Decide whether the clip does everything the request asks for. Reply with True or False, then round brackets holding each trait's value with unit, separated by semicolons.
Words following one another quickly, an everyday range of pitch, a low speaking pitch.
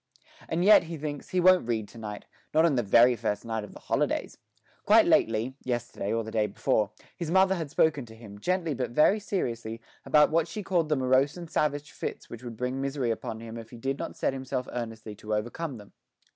False (220 wpm; 5.9 semitones; 130 Hz)